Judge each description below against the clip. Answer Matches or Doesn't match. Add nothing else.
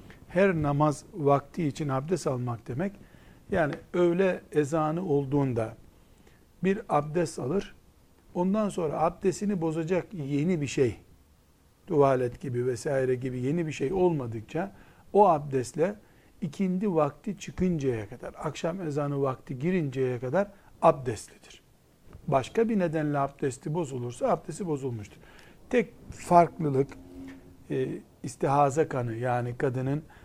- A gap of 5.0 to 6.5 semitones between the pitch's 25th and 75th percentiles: Matches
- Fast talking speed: Doesn't match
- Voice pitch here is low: Doesn't match